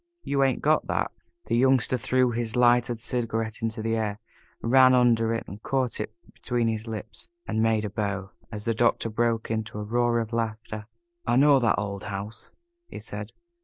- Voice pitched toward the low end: Yes, low, 115 Hz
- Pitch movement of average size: No, narrow, 1.9 semitones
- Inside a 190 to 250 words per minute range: No, average, 180 wpm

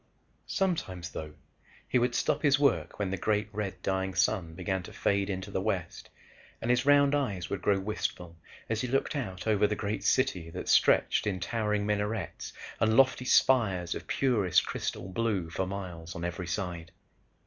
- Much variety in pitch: No, average, 3.9 semitones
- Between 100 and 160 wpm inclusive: No, average, 175 wpm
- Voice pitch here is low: Yes, low, 100 Hz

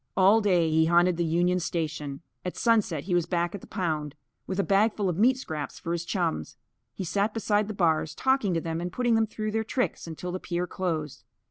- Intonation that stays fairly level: No, average, 4.1 semitones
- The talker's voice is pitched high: No, medium, 180 Hz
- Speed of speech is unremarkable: No, fast, 220 wpm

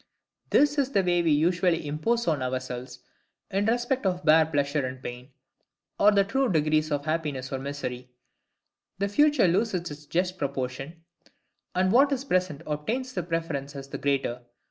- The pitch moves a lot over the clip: Yes, wide, 5.8 semitones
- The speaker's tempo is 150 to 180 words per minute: Yes, average, 165 wpm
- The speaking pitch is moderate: Yes, medium, 160 Hz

